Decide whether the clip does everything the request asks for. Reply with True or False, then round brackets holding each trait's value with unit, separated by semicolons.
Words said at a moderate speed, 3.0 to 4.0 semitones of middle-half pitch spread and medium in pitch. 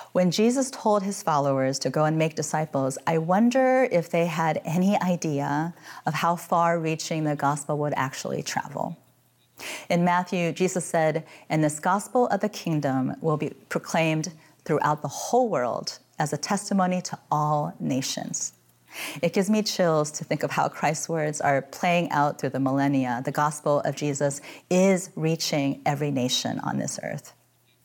True (165 wpm; 3.6 semitones; 160 Hz)